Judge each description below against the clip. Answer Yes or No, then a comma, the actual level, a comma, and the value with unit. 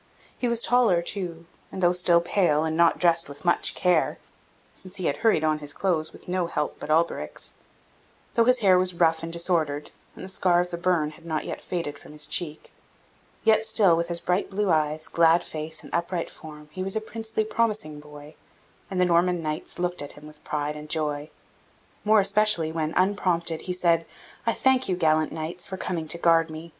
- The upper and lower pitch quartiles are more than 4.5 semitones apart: No, average, 2.9 semitones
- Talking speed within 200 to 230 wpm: Yes, fast, 205 wpm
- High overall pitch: No, medium, 170 Hz